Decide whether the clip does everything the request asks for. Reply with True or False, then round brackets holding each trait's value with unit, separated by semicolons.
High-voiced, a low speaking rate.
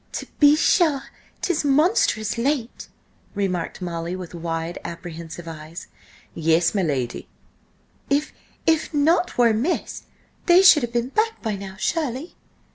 True (225 Hz; 125 wpm)